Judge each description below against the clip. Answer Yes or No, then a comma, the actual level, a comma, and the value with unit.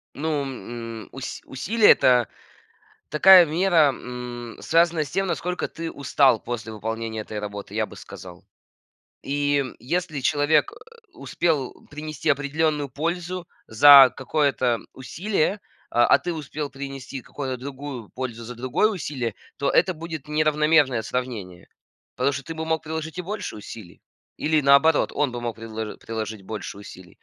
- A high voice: No, medium, 140 Hz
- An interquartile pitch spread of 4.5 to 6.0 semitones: Yes, average, 4.8 semitones